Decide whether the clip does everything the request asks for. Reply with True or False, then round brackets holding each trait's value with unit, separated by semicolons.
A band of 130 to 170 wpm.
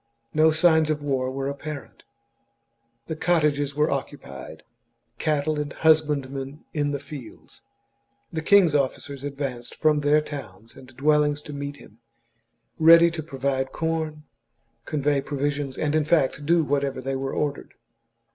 True (150 wpm)